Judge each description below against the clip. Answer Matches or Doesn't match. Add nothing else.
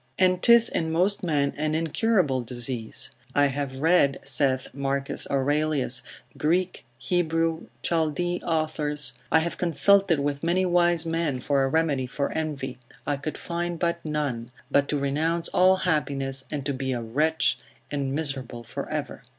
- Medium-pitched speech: Matches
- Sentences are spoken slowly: Doesn't match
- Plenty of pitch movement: Doesn't match